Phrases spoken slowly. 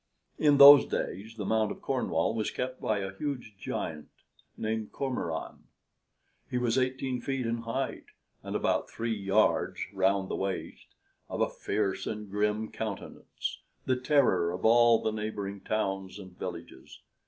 No: average, 150 wpm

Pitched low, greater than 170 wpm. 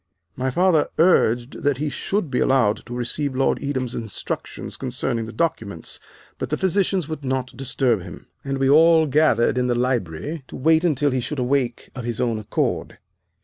Yes: low, 130 Hz; average, 180 wpm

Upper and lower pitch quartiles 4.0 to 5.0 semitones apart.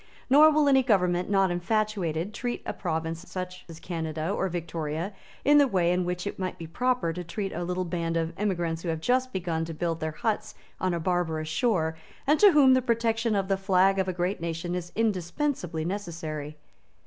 Yes: average, 4.4 semitones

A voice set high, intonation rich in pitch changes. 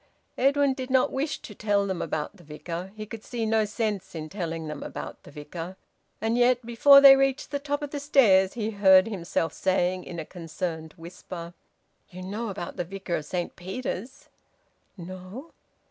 Yes: high, 195 Hz; wide, 5.8 semitones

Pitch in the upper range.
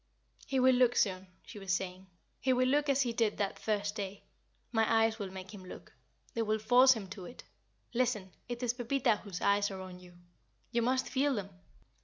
Yes: high, 220 Hz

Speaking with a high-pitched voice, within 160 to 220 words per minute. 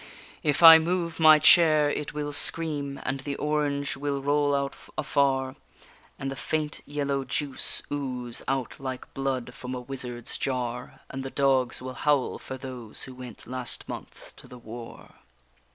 No: low, 135 Hz; average, 165 wpm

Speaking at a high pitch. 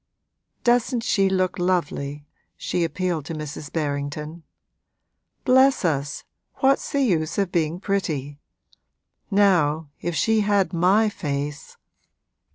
No: medium, 175 Hz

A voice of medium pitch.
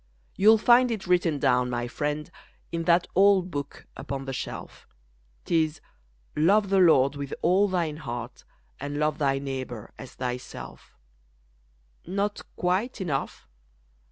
Yes: medium, 155 Hz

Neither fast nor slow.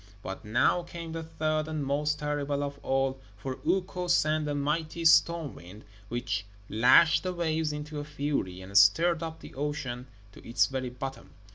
Yes: average, 170 wpm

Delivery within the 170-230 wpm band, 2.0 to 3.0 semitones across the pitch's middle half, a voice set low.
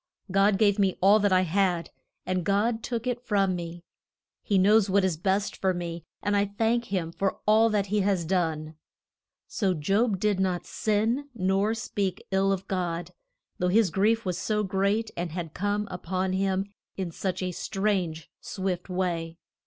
No: average, 175 wpm; narrow, 2.4 semitones; high, 195 Hz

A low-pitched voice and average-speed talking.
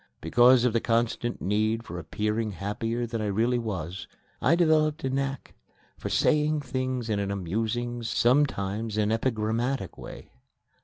Yes: low, 115 Hz; average, 145 wpm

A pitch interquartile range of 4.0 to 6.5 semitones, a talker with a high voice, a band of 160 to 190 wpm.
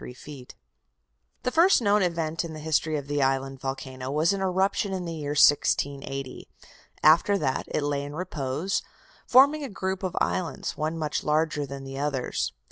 No: average, 4.9 semitones; medium, 155 Hz; average, 165 wpm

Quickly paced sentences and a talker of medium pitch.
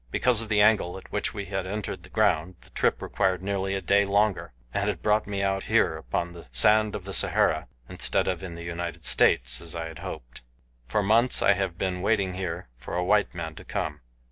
No: fast, 220 wpm; very low, 95 Hz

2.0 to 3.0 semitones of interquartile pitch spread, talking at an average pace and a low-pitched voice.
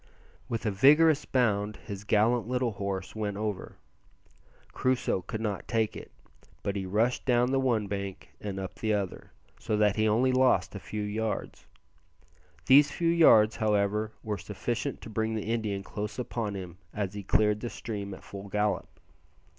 Yes: average, 2.7 semitones; average, 170 wpm; low, 105 Hz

